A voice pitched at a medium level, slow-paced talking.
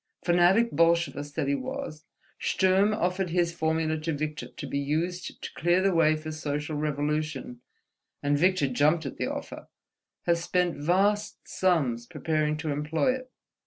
No: medium, 160 Hz; average, 150 wpm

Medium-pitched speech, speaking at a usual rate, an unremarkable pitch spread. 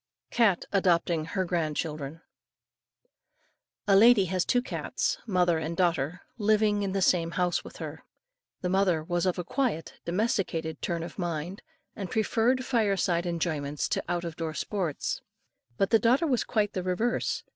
Yes: medium, 180 Hz; average, 160 wpm; average, 3.7 semitones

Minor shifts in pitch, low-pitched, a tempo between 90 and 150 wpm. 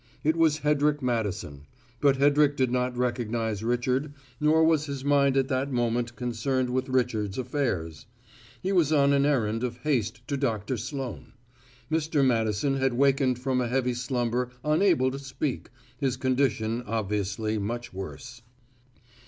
No: average, 3.2 semitones; low, 130 Hz; average, 145 wpm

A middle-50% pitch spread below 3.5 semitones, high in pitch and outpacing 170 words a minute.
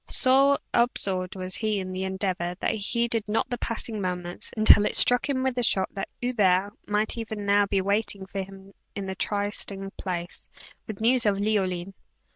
Yes: average, 2.8 semitones; high, 200 Hz; average, 185 wpm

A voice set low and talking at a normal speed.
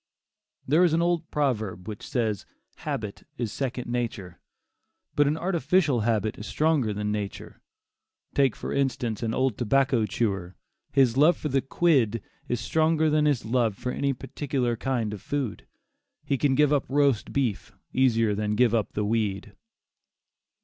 Yes: low, 125 Hz; average, 160 wpm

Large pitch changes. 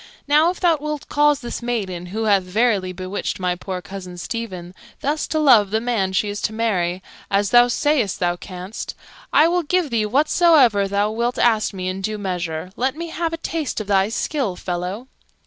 Yes: wide, 6.7 semitones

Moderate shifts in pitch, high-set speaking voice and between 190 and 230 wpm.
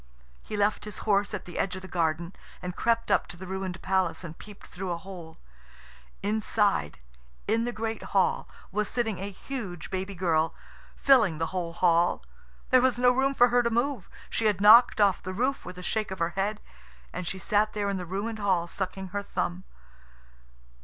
Yes: average, 3.4 semitones; high, 195 Hz; average, 195 wpm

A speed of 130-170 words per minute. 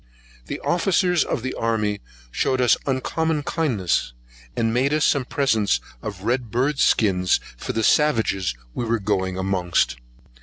Yes: average, 145 wpm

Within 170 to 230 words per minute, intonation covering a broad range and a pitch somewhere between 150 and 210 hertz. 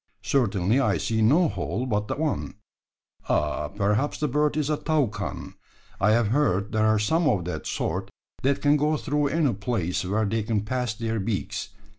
No: average, 180 wpm; wide, 5.9 semitones; low, 115 Hz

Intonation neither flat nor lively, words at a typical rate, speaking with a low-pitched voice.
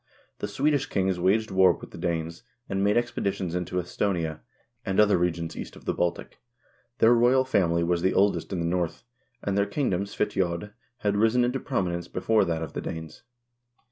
Yes: average, 3.4 semitones; average, 190 wpm; very low, 95 Hz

